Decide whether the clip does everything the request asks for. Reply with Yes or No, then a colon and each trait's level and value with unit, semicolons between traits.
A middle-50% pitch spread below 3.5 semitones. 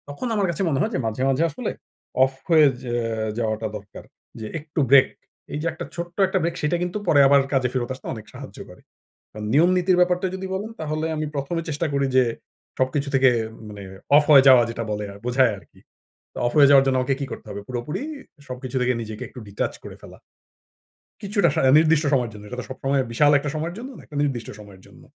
No: average, 4.4 semitones